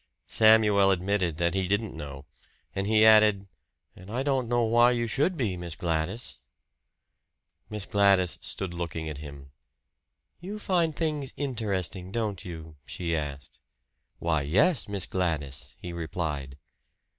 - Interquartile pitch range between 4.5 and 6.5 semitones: Yes, average, 5.3 semitones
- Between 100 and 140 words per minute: Yes, slow, 135 wpm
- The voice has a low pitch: Yes, very low, 95 Hz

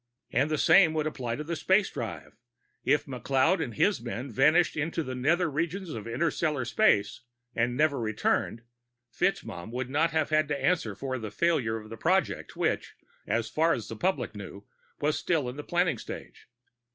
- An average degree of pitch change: No, wide, 5.7 semitones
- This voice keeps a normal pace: Yes, average, 180 wpm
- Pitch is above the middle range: No, medium, 140 Hz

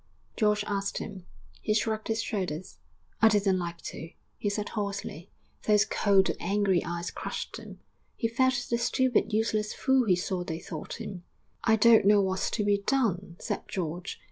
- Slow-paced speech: No, average, 170 wpm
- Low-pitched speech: No, high, 205 Hz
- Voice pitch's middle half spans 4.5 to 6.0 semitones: No, average, 3.1 semitones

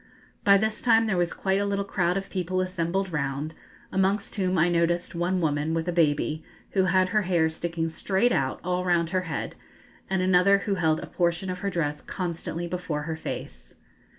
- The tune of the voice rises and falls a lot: No, narrow, 2.6 semitones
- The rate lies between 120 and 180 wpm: No, average, 195 wpm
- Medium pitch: Yes, medium, 180 Hz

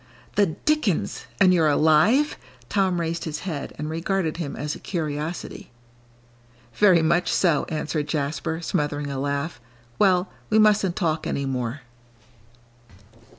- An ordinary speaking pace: No, slow, 130 wpm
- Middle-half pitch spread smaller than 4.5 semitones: Yes, average, 3.8 semitones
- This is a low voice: No, medium, 160 Hz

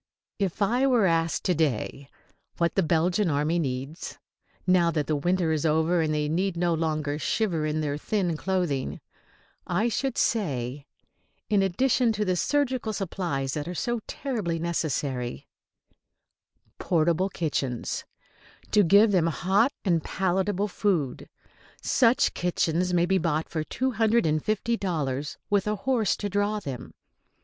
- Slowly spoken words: No, average, 145 wpm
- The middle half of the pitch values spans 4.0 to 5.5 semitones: Yes, average, 4.8 semitones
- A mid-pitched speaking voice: Yes, medium, 175 Hz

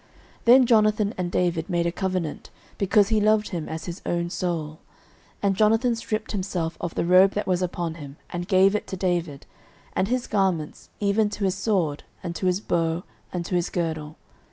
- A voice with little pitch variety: No, average, 3.4 semitones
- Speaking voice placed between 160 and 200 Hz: Yes, medium, 185 Hz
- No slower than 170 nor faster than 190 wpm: No, average, 200 wpm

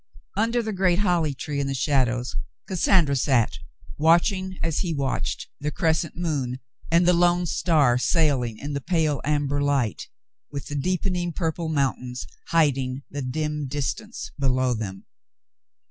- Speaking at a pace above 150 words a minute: No, average, 145 wpm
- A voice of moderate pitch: Yes, medium, 150 Hz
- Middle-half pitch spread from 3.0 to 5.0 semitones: Yes, average, 4.4 semitones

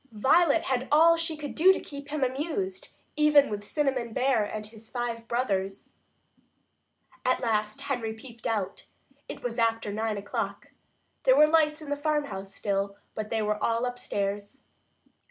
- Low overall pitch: No, high, 245 Hz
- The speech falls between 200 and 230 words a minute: No, average, 155 wpm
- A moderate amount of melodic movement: No, wide, 5.7 semitones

